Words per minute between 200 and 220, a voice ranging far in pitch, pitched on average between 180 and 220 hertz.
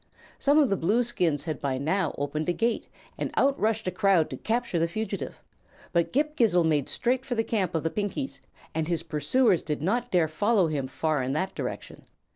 Yes: fast, 205 wpm; wide, 6.5 semitones; medium, 185 Hz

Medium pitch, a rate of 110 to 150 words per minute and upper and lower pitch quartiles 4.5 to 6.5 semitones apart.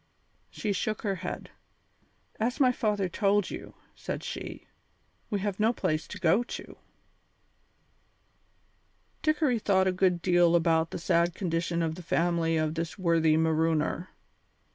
No: medium, 175 Hz; average, 140 wpm; average, 3.7 semitones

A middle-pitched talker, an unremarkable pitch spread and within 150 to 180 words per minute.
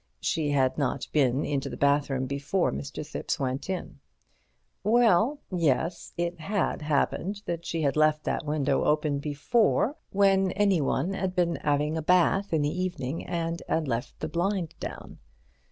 Yes: medium, 160 Hz; average, 4.4 semitones; average, 155 wpm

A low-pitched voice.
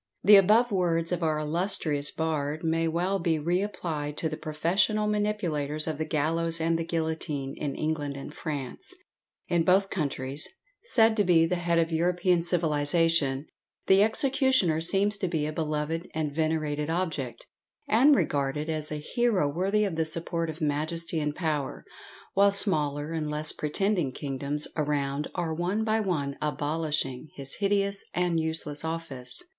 No: medium, 160 Hz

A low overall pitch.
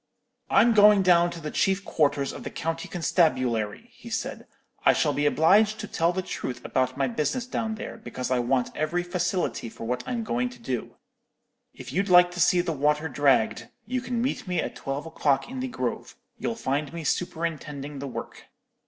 No: medium, 165 Hz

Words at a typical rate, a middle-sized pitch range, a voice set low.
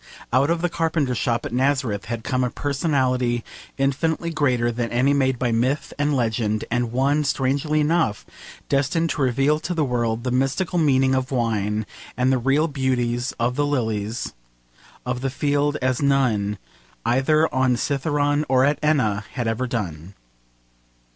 Yes: average, 160 wpm; average, 3.3 semitones; low, 130 Hz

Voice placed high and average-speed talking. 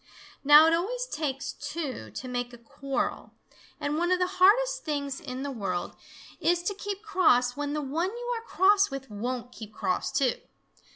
Yes: very high, 295 Hz; average, 180 wpm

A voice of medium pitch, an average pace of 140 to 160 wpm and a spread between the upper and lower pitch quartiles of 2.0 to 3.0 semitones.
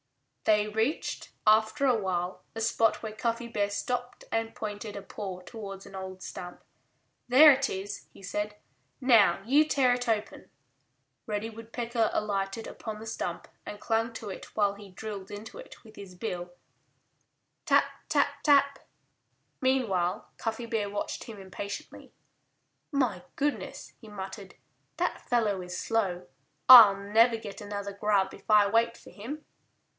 No: high, 215 Hz; average, 150 wpm; average, 2.7 semitones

